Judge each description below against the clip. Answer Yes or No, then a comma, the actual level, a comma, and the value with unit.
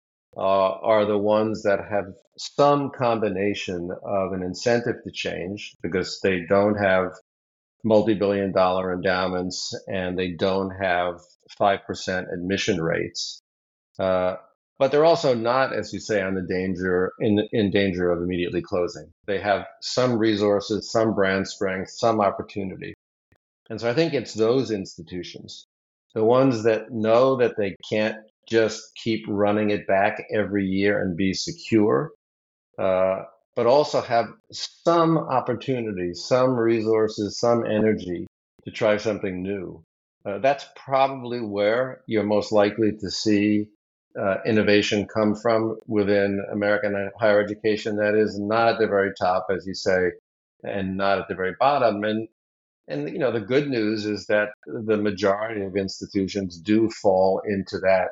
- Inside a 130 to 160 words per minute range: Yes, average, 145 wpm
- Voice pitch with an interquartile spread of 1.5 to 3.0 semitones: Yes, average, 2.7 semitones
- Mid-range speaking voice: No, low, 105 Hz